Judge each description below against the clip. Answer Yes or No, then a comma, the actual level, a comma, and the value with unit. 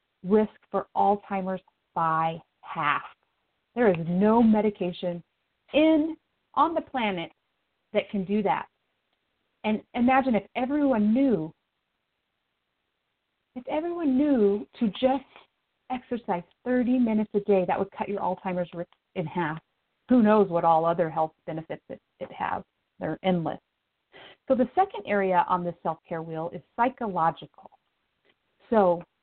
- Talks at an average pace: No, slow, 130 wpm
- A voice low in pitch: No, high, 205 Hz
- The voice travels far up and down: Yes, wide, 6.1 semitones